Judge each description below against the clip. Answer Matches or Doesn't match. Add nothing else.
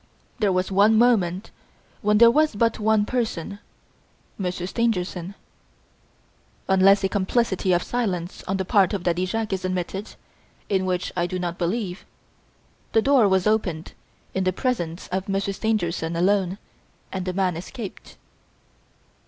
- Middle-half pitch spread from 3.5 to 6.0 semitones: Doesn't match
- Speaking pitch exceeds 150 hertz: Matches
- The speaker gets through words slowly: Doesn't match